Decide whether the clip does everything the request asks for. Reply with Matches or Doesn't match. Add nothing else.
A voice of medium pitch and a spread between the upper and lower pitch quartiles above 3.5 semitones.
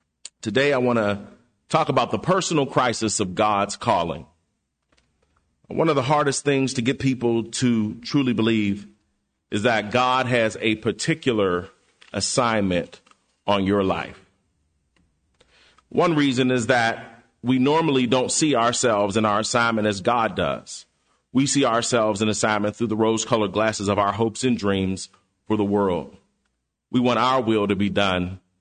Doesn't match